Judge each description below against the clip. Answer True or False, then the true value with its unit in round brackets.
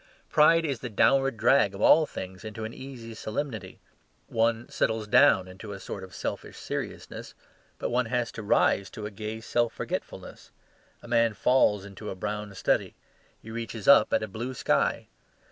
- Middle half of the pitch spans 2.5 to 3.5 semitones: True (2.8 semitones)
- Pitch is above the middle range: False (110 Hz)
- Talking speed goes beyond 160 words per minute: True (175 wpm)